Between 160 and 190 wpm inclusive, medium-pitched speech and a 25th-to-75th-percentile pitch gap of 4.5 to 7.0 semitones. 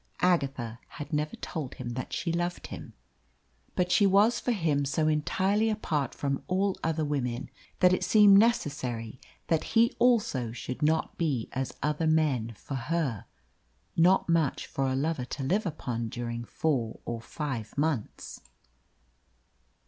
No: average, 150 wpm; medium, 150 Hz; wide, 5.6 semitones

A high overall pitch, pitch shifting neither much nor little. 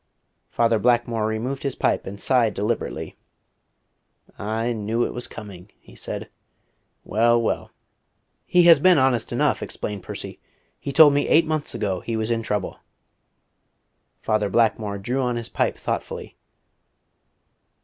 No: low, 115 Hz; average, 3.4 semitones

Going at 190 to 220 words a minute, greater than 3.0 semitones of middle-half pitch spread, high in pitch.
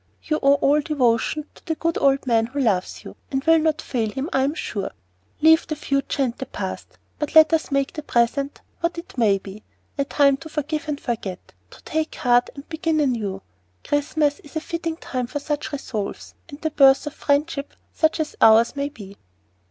Yes: average, 200 wpm; average, 4.0 semitones; very high, 280 Hz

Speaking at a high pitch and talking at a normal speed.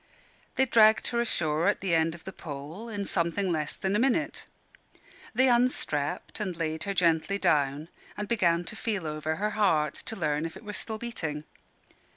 No: medium, 180 Hz; average, 185 wpm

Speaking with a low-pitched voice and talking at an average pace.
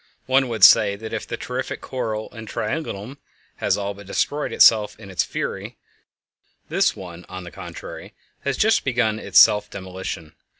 Yes: low, 110 Hz; average, 165 wpm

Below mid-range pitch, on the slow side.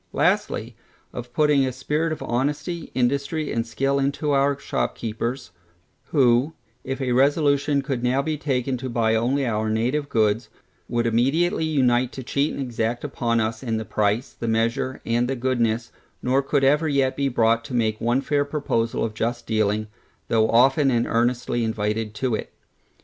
No: low, 125 Hz; average, 170 wpm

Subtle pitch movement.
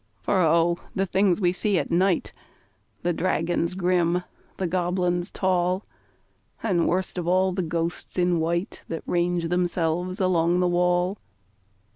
Yes: narrow, 1.2 semitones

